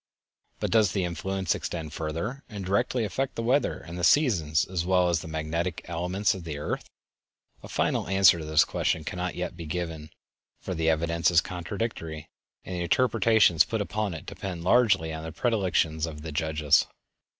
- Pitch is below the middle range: Yes, very low, 85 Hz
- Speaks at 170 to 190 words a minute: Yes, average, 180 wpm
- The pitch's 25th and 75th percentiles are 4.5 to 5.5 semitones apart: No, average, 3.7 semitones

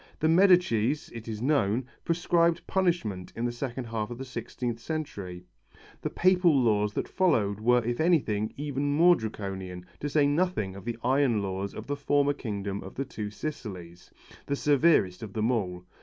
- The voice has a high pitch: No, low, 120 Hz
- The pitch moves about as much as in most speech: No, wide, 6.2 semitones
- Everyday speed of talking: Yes, average, 170 wpm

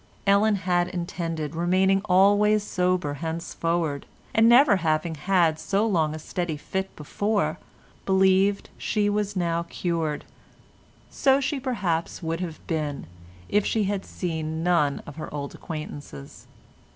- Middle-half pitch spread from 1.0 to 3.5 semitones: No, average, 3.9 semitones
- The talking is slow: Yes, slow, 130 wpm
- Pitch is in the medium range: Yes, medium, 175 Hz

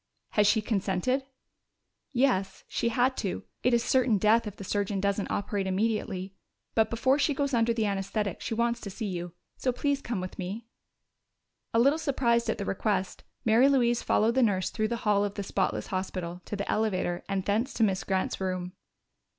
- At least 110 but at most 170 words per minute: No, average, 190 wpm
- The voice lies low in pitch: No, high, 215 Hz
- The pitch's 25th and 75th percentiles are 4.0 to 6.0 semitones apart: No, average, 3.5 semitones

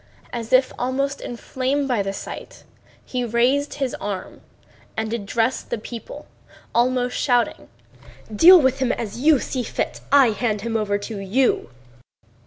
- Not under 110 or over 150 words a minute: Yes, average, 140 wpm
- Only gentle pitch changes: No, average, 3.0 semitones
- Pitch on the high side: Yes, high, 245 Hz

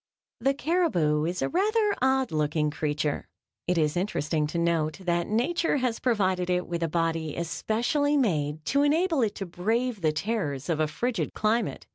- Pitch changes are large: Yes, wide, 8.2 semitones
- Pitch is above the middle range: No, medium, 180 Hz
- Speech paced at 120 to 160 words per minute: No, average, 170 wpm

